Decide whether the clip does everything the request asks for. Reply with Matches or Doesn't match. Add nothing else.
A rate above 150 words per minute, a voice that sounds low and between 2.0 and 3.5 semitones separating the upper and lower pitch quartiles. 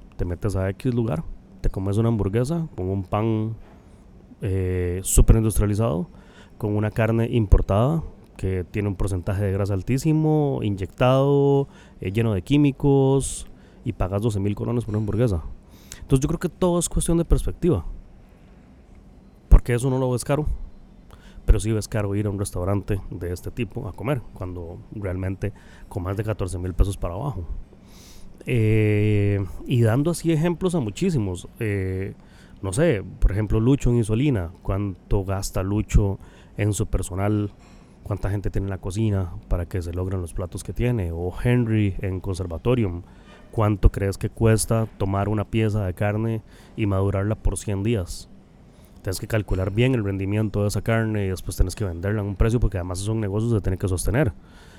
Matches